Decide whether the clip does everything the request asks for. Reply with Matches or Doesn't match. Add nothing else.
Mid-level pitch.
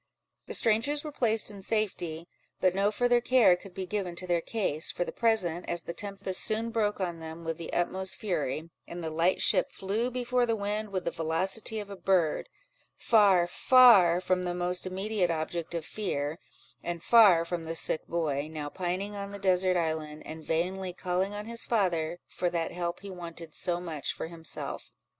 Matches